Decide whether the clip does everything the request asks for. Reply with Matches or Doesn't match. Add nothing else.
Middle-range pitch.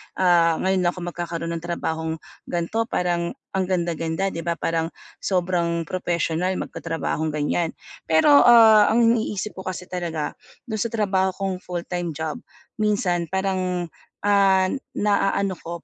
Matches